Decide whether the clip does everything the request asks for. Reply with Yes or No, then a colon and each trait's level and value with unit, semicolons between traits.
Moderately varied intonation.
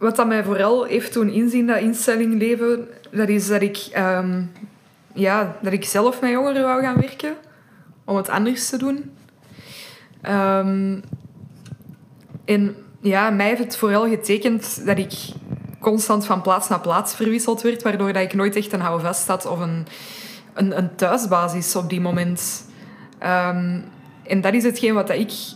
Yes: average, 3.4 semitones